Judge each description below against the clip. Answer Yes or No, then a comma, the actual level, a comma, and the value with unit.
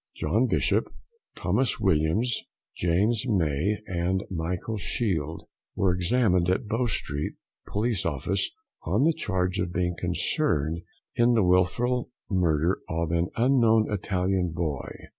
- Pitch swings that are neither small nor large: Yes, average, 4.6 semitones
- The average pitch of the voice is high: No, very low, 90 Hz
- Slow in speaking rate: Yes, slow, 120 wpm